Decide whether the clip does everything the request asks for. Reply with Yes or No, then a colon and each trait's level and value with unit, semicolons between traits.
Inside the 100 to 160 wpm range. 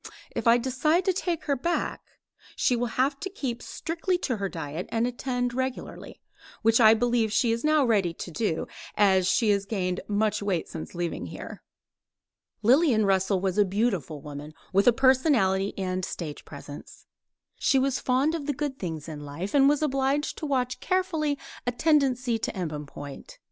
No: average, 175 wpm